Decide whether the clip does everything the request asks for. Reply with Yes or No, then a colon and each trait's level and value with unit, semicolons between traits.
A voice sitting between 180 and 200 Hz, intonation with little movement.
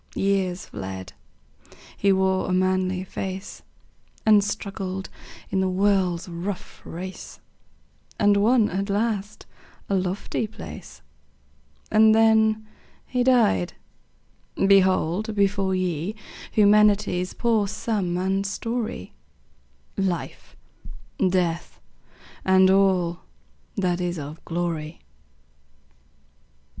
Yes: high, 190 Hz; narrow, 2.3 semitones